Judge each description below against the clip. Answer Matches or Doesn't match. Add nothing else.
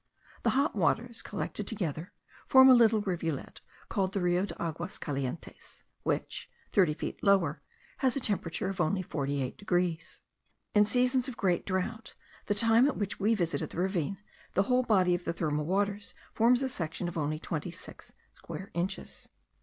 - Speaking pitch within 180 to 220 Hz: Matches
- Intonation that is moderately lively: Matches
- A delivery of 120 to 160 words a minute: Doesn't match